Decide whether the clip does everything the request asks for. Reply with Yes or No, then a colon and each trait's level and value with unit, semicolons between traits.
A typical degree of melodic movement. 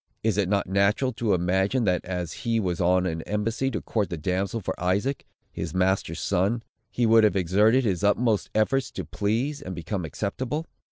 Yes: average, 3.7 semitones